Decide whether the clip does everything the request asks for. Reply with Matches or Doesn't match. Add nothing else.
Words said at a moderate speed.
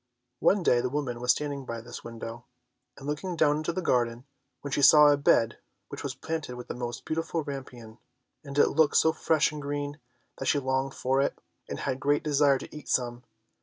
Doesn't match